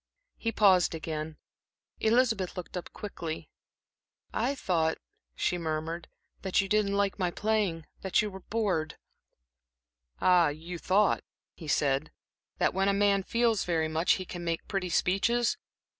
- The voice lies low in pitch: No, medium, 185 Hz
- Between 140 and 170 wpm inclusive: Yes, average, 145 wpm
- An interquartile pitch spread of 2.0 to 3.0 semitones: No, average, 3.8 semitones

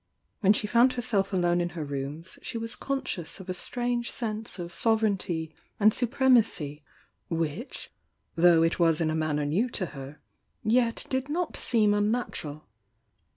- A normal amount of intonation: No, wide, 6.4 semitones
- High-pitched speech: Yes, high, 195 Hz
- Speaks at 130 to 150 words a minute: No, average, 160 wpm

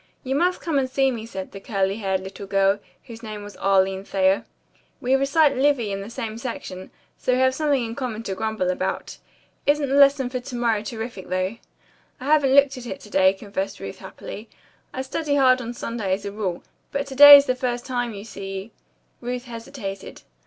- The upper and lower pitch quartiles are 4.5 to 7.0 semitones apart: Yes, average, 5.1 semitones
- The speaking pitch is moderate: No, high, 230 Hz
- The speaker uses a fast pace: Yes, fast, 210 wpm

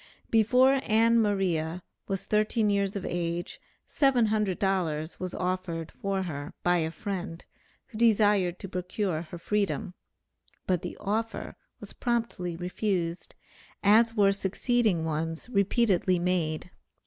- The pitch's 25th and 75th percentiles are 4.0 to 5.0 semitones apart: No, average, 3.6 semitones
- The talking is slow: Yes, slow, 120 wpm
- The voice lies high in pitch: Yes, high, 195 Hz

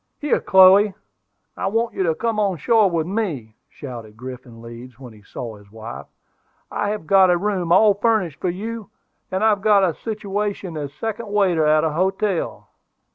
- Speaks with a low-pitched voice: No, medium, 185 Hz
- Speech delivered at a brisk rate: No, average, 180 wpm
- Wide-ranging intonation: Yes, wide, 6.5 semitones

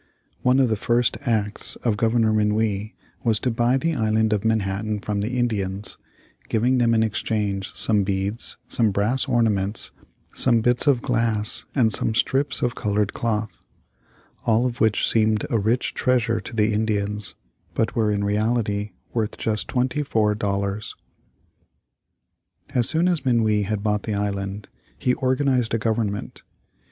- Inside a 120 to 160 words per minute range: Yes, average, 150 wpm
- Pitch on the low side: Yes, low, 110 Hz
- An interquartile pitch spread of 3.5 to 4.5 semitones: No, narrow, 2.4 semitones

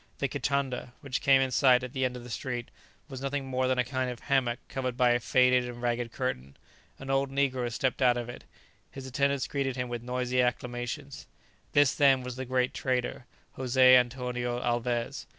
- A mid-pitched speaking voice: No, low, 125 Hz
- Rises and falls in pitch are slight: Yes, narrow, 1.5 semitones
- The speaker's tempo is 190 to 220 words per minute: Yes, average, 195 wpm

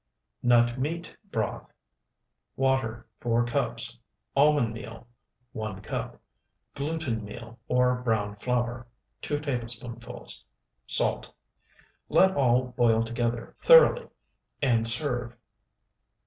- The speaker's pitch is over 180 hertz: No, low, 120 Hz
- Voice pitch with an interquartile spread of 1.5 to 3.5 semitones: Yes, narrow, 2.6 semitones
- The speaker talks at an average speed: No, slow, 90 wpm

